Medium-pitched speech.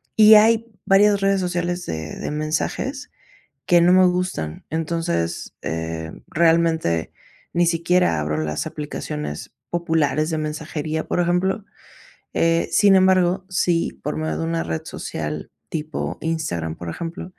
Yes: medium, 165 Hz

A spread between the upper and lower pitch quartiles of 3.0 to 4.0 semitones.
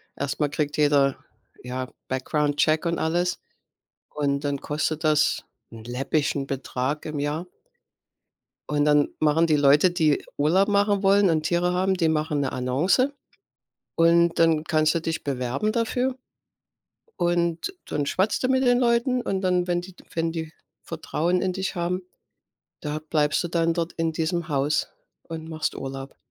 Yes: average, 3.3 semitones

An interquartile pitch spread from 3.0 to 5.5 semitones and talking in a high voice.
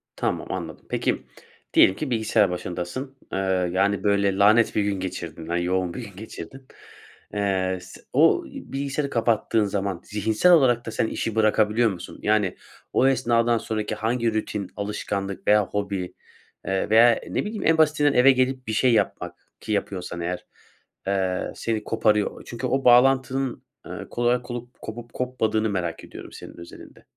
No: average, 4.0 semitones; low, 110 Hz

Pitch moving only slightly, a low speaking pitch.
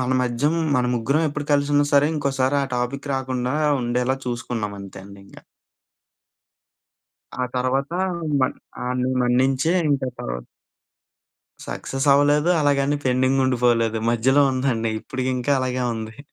Yes: narrow, 2.3 semitones; low, 130 Hz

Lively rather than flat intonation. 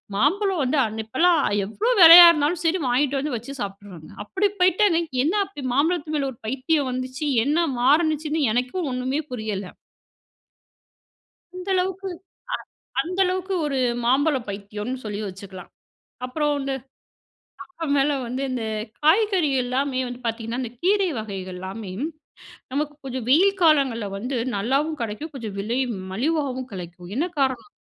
Yes: wide, 5.9 semitones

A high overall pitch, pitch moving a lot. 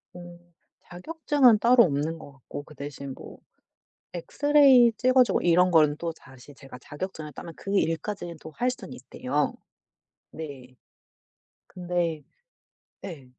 No: medium, 170 Hz; wide, 6.4 semitones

